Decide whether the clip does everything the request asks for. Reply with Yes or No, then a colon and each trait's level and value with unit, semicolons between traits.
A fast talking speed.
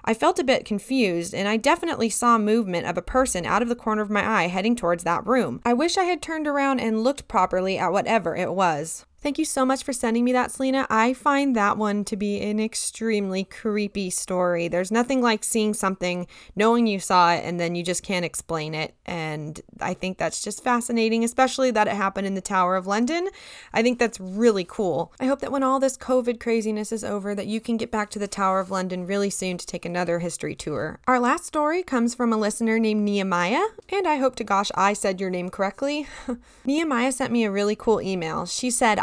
Yes: fast, 225 wpm